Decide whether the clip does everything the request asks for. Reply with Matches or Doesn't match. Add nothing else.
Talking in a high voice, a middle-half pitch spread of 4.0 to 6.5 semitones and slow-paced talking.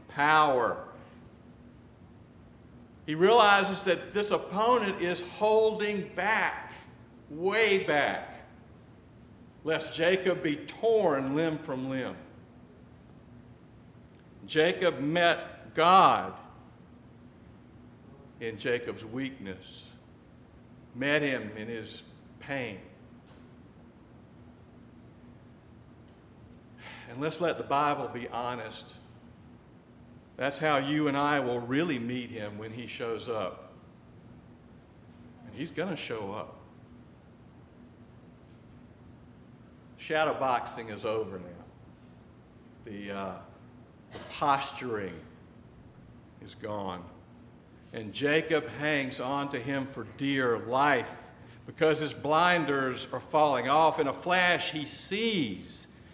Doesn't match